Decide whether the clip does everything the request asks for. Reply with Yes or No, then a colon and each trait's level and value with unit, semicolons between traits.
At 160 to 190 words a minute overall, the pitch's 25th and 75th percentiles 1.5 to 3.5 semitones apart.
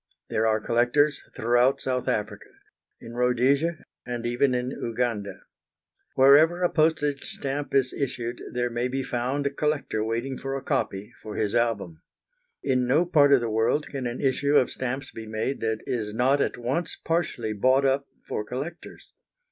Yes: average, 165 wpm; average, 3.1 semitones